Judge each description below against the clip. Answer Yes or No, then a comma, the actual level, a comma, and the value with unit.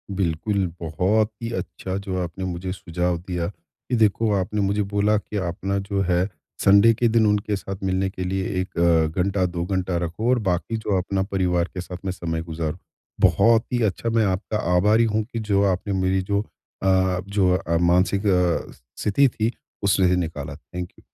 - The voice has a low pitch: Yes, very low, 95 Hz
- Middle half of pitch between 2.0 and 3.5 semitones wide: Yes, narrow, 2.5 semitones